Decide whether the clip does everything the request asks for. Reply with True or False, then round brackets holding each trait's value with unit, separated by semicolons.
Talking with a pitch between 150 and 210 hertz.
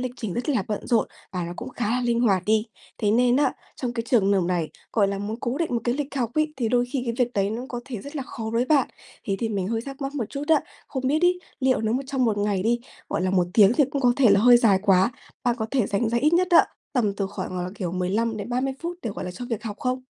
False (235 Hz)